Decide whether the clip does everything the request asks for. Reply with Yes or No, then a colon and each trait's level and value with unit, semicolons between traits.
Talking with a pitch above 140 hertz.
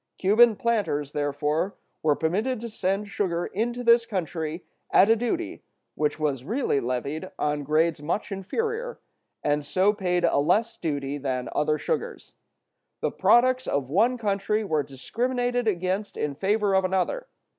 Yes: high, 190 Hz